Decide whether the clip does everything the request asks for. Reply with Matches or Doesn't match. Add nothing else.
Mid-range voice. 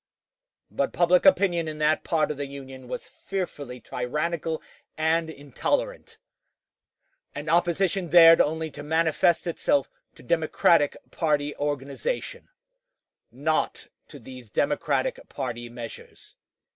Matches